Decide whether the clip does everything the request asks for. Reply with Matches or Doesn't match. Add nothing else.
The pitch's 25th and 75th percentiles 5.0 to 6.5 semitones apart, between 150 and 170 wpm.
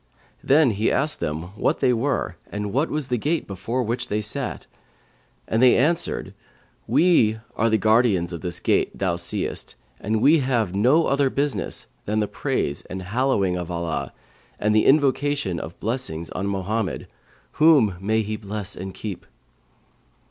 Matches